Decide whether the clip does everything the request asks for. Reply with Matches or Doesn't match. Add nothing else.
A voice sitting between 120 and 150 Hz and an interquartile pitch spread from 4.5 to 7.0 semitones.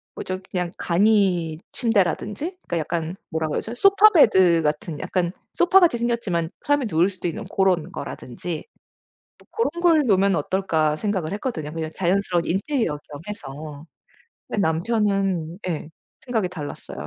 Doesn't match